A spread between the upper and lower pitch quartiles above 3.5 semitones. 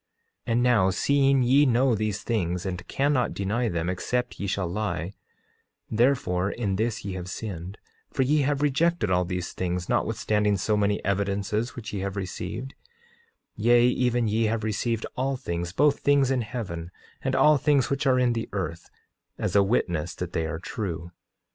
Yes: average, 5.3 semitones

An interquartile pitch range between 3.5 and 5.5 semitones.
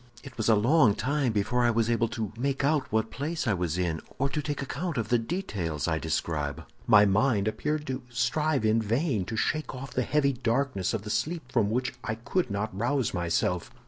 Yes: average, 5.1 semitones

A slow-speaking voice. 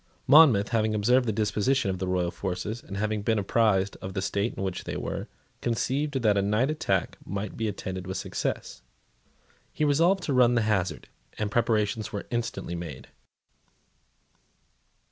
No: average, 165 wpm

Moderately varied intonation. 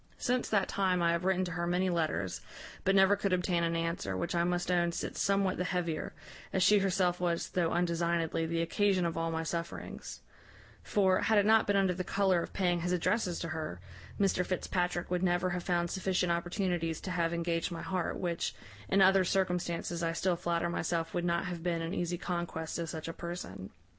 No: narrow, 1.8 semitones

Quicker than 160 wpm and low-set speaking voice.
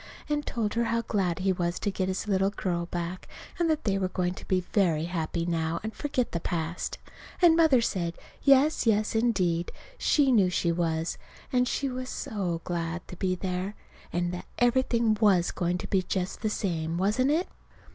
No: average, 190 wpm; high, 190 Hz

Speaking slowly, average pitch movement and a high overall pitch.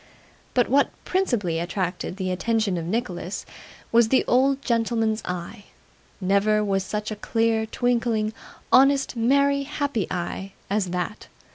Yes: slow, 130 wpm; average, 4.2 semitones; high, 220 Hz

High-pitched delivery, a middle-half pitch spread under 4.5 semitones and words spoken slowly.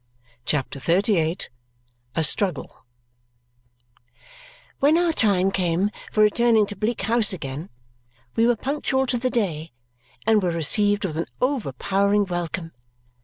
No: high, 200 Hz; average, 5.2 semitones; slow, 120 wpm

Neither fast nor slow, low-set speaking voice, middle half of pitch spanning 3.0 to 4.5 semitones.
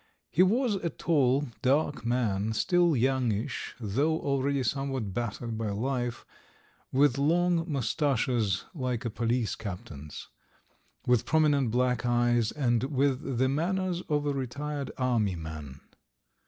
No: slow, 125 wpm; low, 130 Hz; average, 4.1 semitones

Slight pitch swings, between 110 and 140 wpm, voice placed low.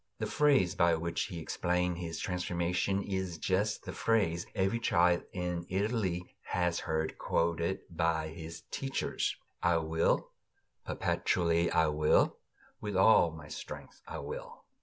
Yes: narrow, 2.3 semitones; slow, 135 wpm; very low, 85 Hz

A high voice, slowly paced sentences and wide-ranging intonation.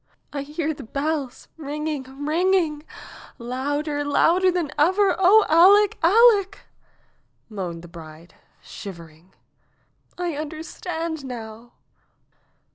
Yes: very high, 300 Hz; slow, 110 wpm; wide, 5.8 semitones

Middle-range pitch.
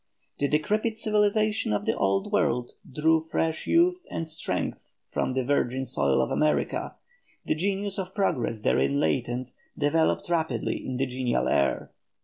Yes: medium, 150 Hz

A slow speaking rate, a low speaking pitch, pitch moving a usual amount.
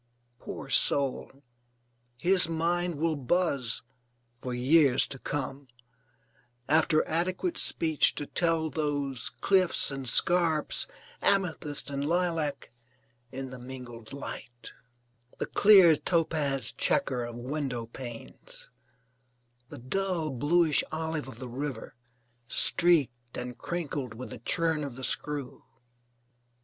No: slow, 110 wpm; medium, 145 Hz; average, 4.4 semitones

